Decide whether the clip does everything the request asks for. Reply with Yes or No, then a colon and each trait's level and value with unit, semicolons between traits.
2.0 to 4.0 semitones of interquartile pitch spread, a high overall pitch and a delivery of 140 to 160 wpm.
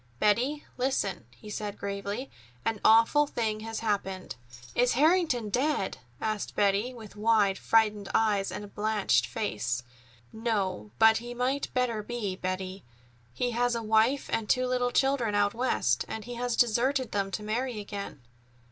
Yes: average, 3.3 semitones; high, 220 Hz; average, 150 wpm